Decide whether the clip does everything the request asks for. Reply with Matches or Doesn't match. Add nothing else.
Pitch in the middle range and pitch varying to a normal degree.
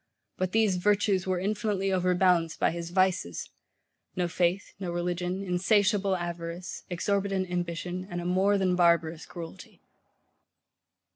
Doesn't match